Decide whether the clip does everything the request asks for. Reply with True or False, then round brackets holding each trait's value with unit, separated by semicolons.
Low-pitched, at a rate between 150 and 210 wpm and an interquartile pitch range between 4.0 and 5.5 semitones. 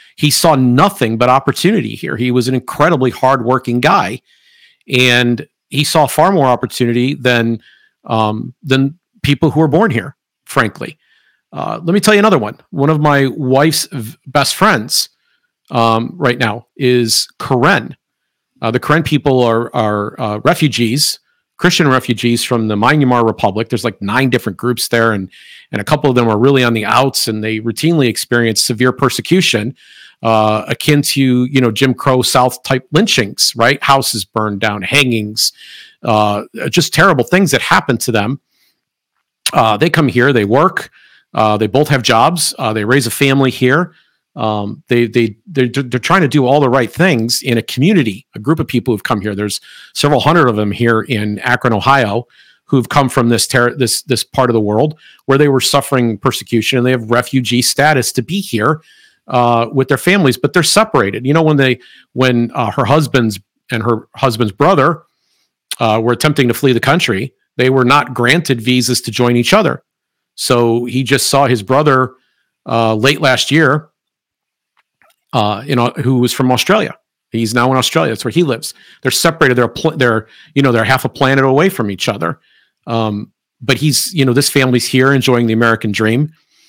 False (125 Hz; 185 wpm; 3.4 semitones)